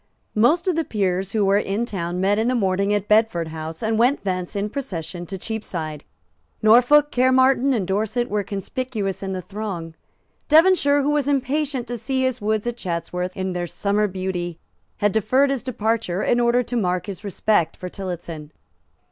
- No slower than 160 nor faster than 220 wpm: Yes, average, 180 wpm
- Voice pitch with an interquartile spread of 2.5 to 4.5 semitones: No, average, 5.1 semitones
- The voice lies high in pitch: Yes, high, 210 Hz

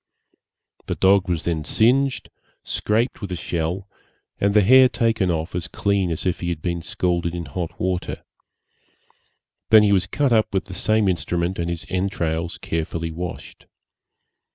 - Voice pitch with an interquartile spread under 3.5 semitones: Yes, average, 3.0 semitones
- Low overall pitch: Yes, very low, 90 Hz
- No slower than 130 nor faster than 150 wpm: No, average, 160 wpm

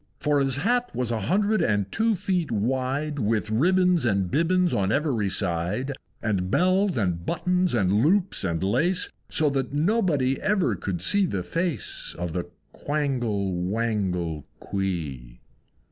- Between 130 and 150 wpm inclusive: Yes, average, 145 wpm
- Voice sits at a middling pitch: No, low, 125 Hz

